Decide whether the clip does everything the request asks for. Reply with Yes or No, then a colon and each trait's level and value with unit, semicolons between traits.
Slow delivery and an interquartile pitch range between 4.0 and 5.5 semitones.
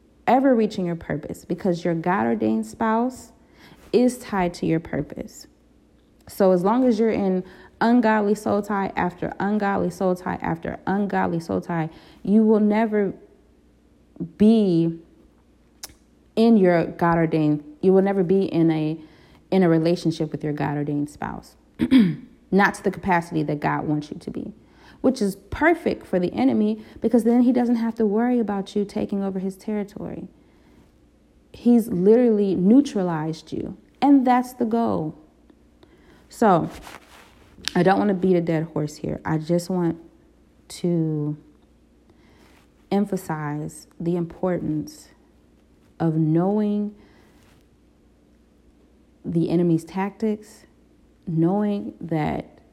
Yes: slow, 130 wpm; average, 5.1 semitones